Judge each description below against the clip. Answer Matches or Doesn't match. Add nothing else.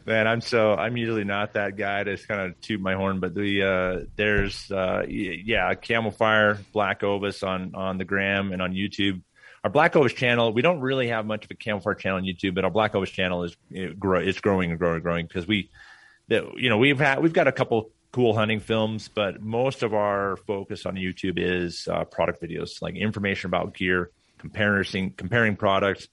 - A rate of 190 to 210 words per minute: Matches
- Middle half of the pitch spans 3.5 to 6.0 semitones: Doesn't match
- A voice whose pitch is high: Doesn't match